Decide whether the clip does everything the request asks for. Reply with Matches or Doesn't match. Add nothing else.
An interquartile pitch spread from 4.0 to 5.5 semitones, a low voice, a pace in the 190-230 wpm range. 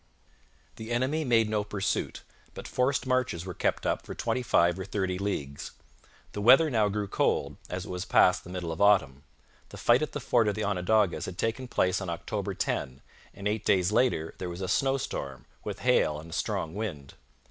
Matches